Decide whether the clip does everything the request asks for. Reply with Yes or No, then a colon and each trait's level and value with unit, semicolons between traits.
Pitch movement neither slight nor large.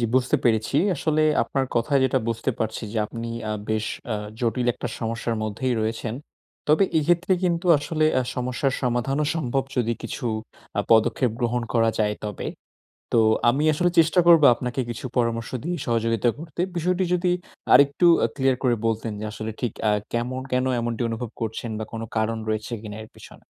Yes: average, 3.8 semitones